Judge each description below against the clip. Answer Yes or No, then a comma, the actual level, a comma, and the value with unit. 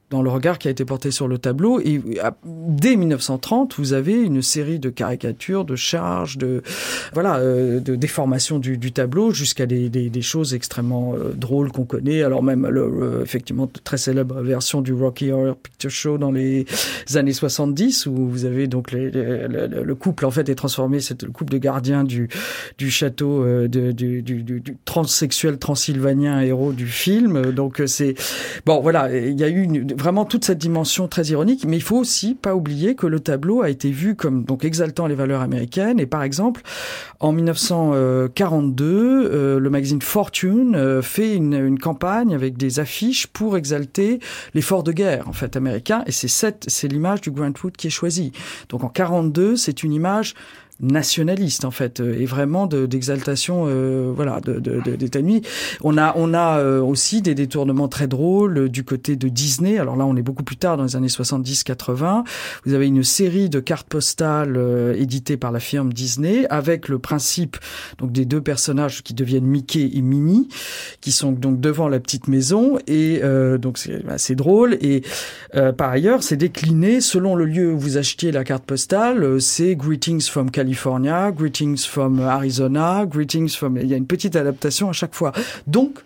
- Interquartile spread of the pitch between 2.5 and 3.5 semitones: No, average, 4.3 semitones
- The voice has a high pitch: No, medium, 140 Hz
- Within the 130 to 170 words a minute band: No, average, 190 wpm